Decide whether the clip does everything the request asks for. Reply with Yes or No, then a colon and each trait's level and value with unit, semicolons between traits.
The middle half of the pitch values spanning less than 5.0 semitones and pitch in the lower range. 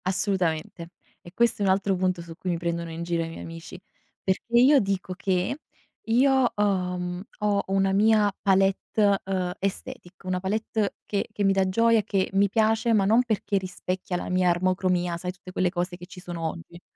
No: narrow, 2.4 semitones; high, 190 Hz